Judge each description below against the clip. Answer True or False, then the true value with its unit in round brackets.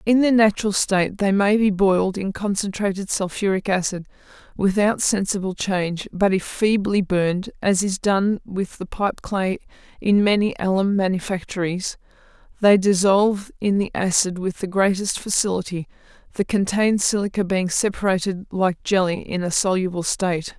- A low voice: False (195 Hz)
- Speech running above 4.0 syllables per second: True (5.0 syllables/s)